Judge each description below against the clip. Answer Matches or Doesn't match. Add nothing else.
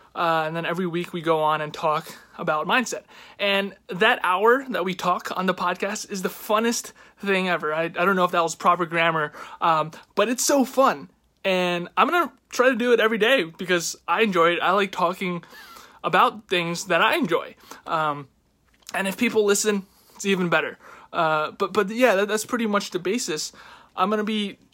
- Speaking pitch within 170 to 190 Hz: Matches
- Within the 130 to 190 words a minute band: Doesn't match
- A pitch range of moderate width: Matches